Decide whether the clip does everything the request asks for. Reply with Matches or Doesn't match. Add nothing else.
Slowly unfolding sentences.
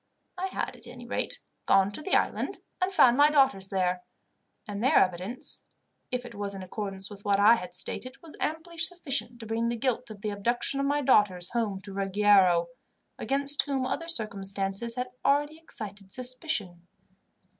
Doesn't match